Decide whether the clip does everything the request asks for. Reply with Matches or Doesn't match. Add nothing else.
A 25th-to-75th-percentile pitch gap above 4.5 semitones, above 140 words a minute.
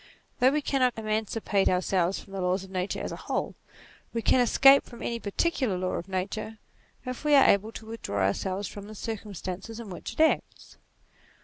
Doesn't match